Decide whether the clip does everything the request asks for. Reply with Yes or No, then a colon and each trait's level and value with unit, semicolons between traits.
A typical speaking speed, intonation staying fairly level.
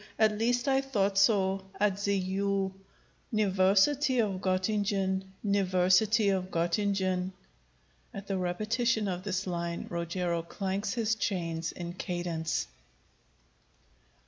No: slow, 110 wpm; narrow, 2.3 semitones